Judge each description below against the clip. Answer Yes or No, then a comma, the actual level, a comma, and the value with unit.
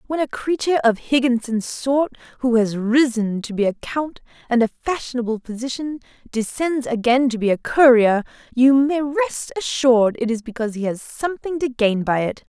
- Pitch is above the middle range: Yes, very high, 250 Hz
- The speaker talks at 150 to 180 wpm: Yes, average, 175 wpm